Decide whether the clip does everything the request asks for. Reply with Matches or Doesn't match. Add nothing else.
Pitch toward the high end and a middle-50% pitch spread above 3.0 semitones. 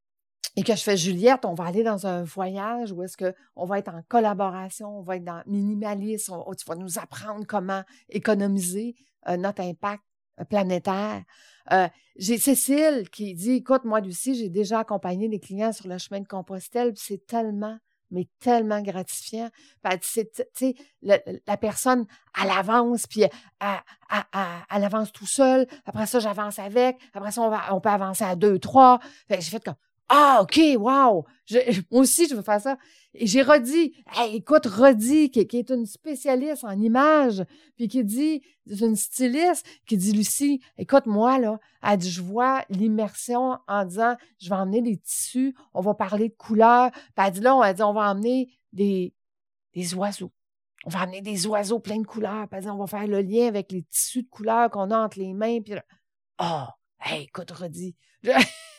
Matches